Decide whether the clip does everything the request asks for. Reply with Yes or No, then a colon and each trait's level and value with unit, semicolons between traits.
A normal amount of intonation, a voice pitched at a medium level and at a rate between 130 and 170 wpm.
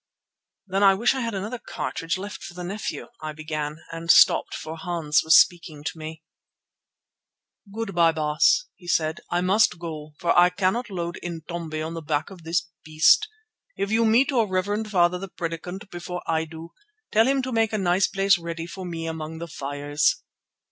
No: average, 3.5 semitones; medium, 175 Hz; average, 185 wpm